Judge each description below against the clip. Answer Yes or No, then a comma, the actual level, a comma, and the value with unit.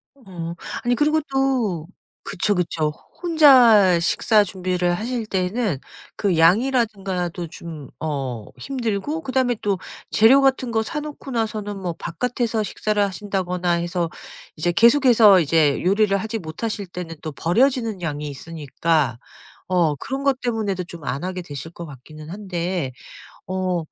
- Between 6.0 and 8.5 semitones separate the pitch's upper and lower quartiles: No, wide, 5.5 semitones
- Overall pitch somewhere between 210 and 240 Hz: No, high, 190 Hz